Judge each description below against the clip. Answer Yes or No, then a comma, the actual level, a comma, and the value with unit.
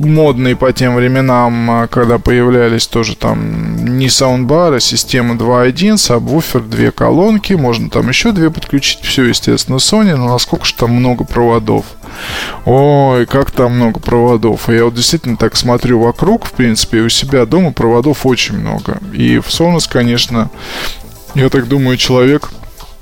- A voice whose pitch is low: Yes, low, 125 Hz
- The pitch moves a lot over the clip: No, average, 2.9 semitones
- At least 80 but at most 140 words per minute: No, average, 155 wpm